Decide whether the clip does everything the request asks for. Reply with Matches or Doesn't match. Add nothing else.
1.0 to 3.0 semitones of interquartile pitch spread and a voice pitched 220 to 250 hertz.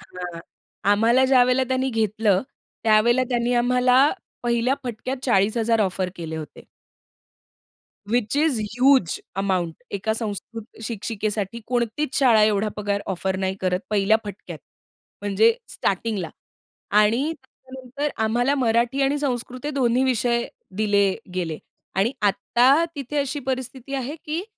Doesn't match